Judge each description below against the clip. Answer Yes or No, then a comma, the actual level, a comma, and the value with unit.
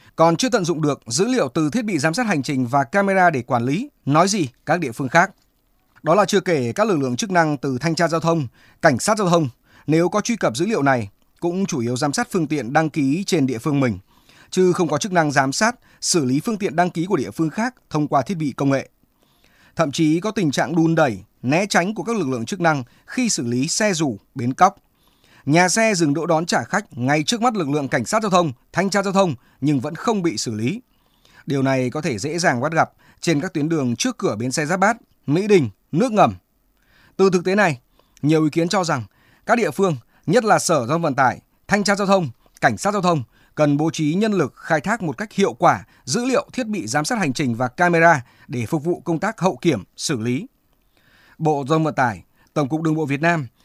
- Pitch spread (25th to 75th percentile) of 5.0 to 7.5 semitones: Yes, wide, 5.4 semitones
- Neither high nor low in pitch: Yes, medium, 160 Hz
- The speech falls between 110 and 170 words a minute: No, fast, 250 wpm